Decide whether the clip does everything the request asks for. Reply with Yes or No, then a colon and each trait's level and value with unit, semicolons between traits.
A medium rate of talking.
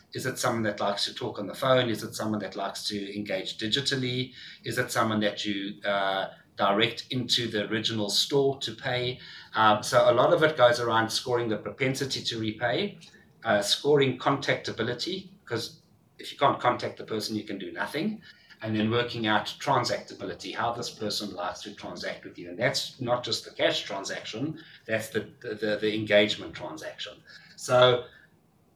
Yes: average, 175 wpm